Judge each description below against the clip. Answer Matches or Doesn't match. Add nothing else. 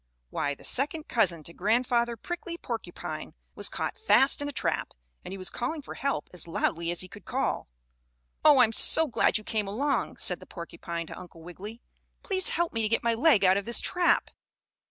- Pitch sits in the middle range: Doesn't match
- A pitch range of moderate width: Doesn't match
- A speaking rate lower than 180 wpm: Doesn't match